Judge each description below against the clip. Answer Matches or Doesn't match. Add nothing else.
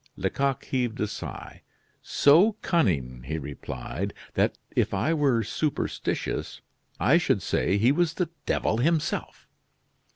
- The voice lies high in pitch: Doesn't match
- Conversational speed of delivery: Doesn't match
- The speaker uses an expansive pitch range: Matches